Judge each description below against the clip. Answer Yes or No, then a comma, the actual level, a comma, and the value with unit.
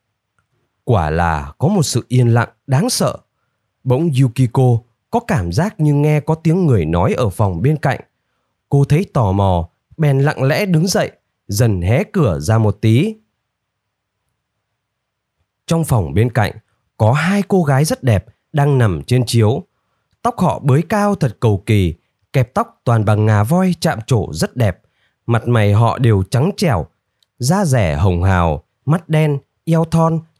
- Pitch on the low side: Yes, low, 125 Hz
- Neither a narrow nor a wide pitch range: No, wide, 6.2 semitones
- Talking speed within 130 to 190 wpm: Yes, slow, 165 wpm